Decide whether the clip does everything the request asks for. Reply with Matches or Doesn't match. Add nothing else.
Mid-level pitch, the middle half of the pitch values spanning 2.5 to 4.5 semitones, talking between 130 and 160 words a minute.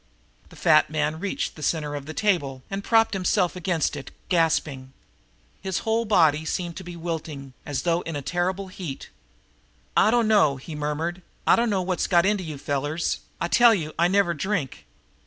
Doesn't match